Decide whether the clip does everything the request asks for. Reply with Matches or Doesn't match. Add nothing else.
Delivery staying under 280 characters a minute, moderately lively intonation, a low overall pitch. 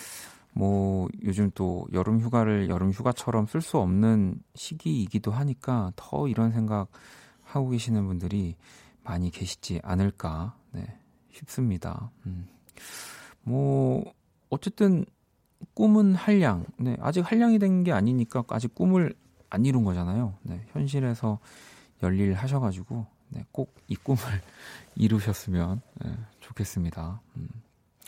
Doesn't match